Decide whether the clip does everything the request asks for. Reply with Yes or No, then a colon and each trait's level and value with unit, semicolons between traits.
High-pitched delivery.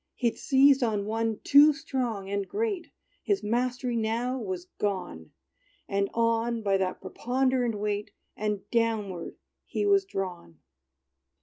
Yes: high, 225 Hz